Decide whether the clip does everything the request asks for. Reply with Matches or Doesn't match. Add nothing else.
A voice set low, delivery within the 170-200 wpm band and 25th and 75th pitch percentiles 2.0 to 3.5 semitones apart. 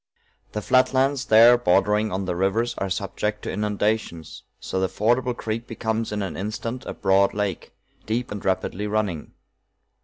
Doesn't match